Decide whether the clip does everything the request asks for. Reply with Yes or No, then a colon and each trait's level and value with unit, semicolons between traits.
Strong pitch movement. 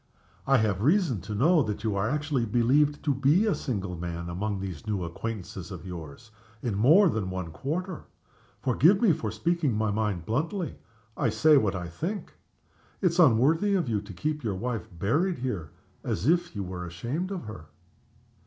Yes: wide, 8.0 semitones